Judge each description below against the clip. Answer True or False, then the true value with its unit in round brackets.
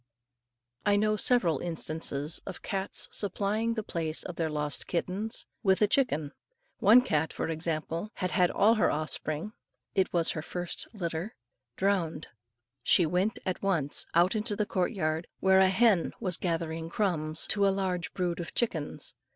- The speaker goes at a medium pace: True (160 wpm)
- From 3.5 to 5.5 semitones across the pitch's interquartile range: True (3.9 semitones)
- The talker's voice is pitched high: False (180 Hz)